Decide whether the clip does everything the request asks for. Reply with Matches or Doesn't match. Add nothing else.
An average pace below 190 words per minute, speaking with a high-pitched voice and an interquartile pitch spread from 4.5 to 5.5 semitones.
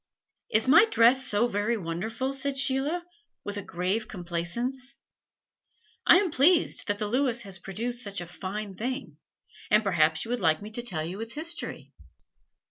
Matches